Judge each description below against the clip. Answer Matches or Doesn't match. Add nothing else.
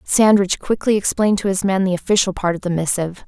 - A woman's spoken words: Matches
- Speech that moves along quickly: Matches